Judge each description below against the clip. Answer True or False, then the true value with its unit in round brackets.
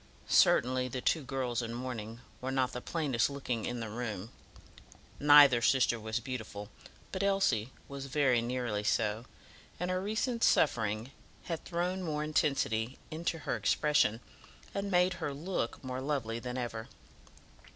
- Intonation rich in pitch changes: False (4.7 semitones)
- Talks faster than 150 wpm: False (145 wpm)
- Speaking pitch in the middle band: False (130 Hz)